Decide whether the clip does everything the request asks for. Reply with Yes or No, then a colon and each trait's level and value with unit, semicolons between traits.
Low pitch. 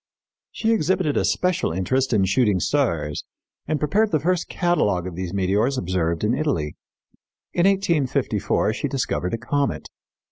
Yes: low, 130 Hz